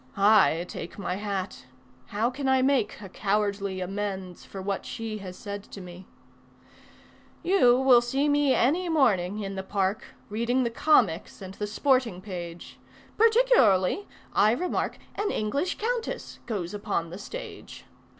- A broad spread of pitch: Yes, wide, 5.7 semitones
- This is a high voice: Yes, high, 210 Hz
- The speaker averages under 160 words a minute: Yes, average, 145 wpm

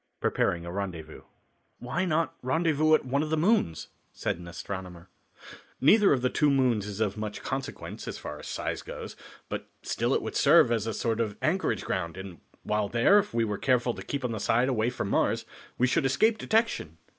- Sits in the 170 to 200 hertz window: No, low, 120 Hz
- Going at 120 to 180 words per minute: No, average, 200 wpm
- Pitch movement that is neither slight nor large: No, wide, 7.0 semitones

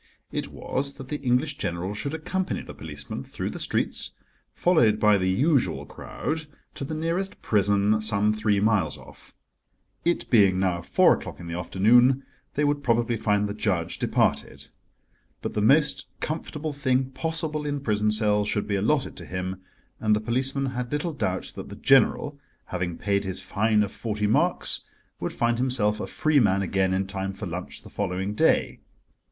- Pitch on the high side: No, low, 110 Hz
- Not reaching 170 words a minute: No, average, 175 wpm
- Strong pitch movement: Yes, wide, 5.8 semitones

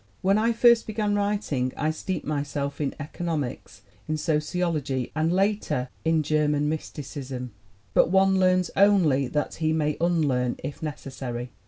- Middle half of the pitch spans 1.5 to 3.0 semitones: No, average, 4.6 semitones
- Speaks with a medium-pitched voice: Yes, medium, 155 Hz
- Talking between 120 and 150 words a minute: Yes, average, 145 wpm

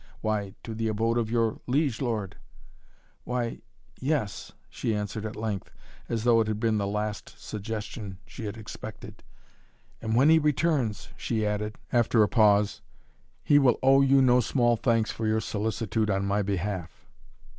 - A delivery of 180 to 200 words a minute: No, average, 165 wpm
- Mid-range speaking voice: No, low, 110 Hz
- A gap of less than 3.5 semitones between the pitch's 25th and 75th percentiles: Yes, narrow, 2.4 semitones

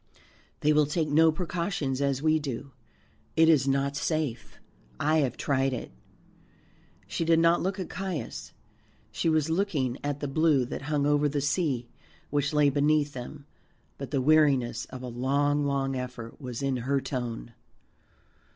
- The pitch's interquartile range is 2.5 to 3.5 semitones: Yes, average, 2.8 semitones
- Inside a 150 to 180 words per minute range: Yes, average, 160 wpm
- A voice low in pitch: No, medium, 145 Hz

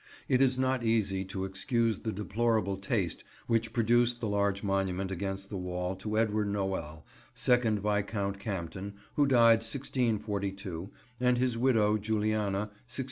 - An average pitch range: Yes, average, 3.0 semitones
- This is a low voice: Yes, low, 105 Hz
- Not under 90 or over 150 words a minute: Yes, average, 140 wpm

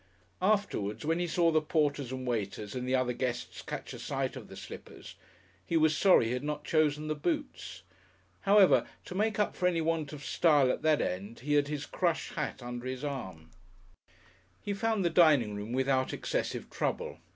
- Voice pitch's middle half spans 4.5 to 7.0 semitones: Yes, average, 4.9 semitones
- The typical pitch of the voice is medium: Yes, medium, 150 Hz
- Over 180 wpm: Yes, average, 190 wpm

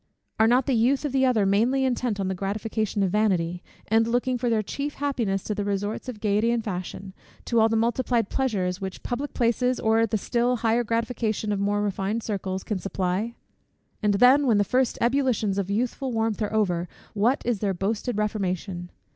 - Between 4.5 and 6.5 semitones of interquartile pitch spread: No, average, 3.3 semitones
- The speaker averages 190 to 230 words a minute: Yes, average, 195 wpm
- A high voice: Yes, high, 220 Hz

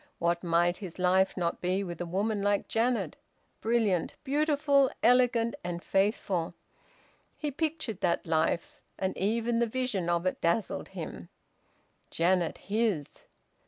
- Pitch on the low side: No, high, 195 Hz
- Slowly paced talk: Yes, slow, 130 wpm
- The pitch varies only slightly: No, average, 5.2 semitones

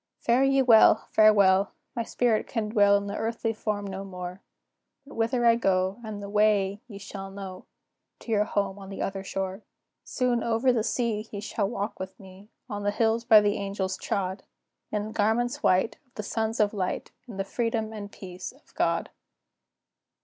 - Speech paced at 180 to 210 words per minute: Yes, average, 185 wpm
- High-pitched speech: Yes, high, 210 Hz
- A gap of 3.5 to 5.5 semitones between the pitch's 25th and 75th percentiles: No, narrow, 2.5 semitones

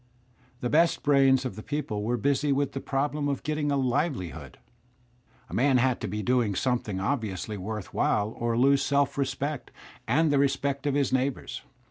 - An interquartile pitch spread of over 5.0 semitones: No, average, 3.6 semitones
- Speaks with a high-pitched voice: No, low, 135 Hz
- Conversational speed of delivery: Yes, average, 175 wpm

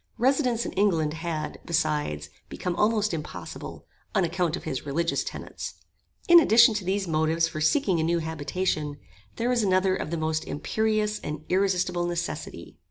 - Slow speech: No, average, 160 wpm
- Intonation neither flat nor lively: Yes, average, 4.7 semitones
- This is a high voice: No, medium, 170 Hz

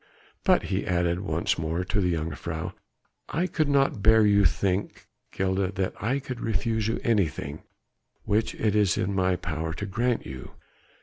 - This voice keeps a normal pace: Yes, average, 170 wpm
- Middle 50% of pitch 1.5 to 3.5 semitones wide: No, average, 4.1 semitones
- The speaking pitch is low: Yes, very low, 95 Hz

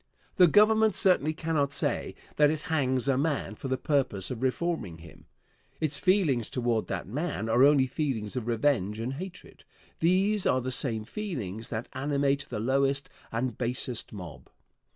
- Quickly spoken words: No, average, 160 wpm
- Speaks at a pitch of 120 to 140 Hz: Yes, low, 135 Hz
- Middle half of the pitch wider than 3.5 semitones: Yes, average, 5.1 semitones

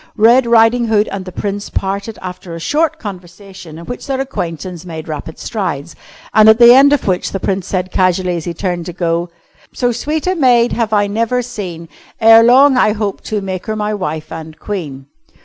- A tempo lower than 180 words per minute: No, average, 200 wpm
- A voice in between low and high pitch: No, high, 200 Hz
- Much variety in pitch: No, average, 4.8 semitones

